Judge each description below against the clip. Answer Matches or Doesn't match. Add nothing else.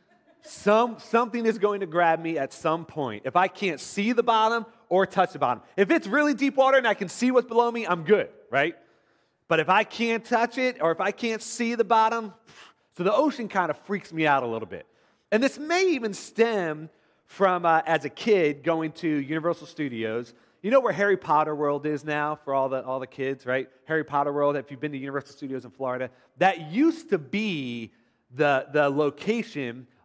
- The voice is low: Doesn't match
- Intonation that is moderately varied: Doesn't match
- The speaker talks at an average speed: Doesn't match